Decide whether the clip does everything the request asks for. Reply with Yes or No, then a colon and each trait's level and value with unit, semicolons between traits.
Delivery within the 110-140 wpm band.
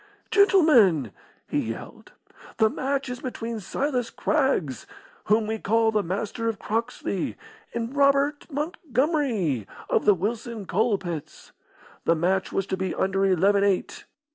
Yes: slow, 135 wpm